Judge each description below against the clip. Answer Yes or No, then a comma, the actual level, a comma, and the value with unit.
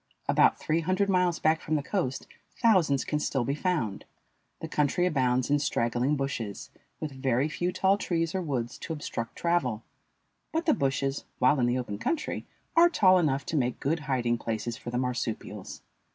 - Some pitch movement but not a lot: No, wide, 5.7 semitones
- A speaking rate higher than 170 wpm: Yes, average, 180 wpm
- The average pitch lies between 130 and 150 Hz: Yes, medium, 140 Hz